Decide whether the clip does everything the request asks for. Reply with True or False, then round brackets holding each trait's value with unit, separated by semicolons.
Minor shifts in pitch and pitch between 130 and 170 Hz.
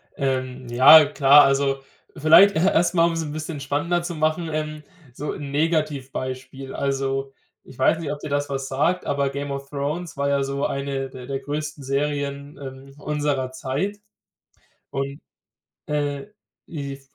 True (2.0 semitones; 140 Hz)